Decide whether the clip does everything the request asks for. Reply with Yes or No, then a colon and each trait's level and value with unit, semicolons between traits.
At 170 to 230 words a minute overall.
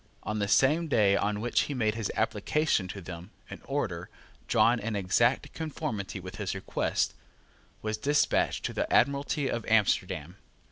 No: average, 155 wpm